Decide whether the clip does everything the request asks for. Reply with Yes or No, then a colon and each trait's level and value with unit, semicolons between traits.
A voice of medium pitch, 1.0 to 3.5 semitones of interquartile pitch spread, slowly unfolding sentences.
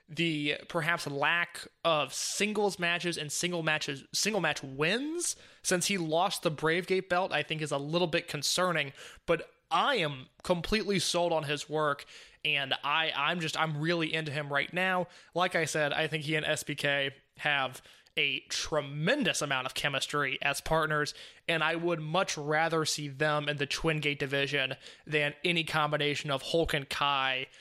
No: medium, 155 Hz; average, 2.9 semitones; average, 170 wpm